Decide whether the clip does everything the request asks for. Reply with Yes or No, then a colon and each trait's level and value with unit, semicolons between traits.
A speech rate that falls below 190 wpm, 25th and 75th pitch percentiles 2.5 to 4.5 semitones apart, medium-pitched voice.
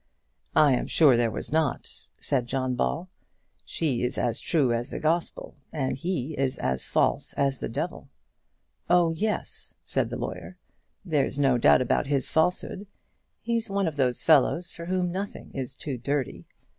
No: average, 165 wpm; average, 4.9 semitones; medium, 145 Hz